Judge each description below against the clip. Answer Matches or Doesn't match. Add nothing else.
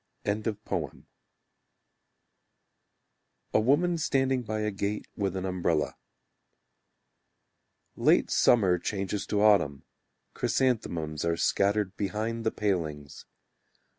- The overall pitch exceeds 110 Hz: Doesn't match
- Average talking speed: Doesn't match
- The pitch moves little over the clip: Doesn't match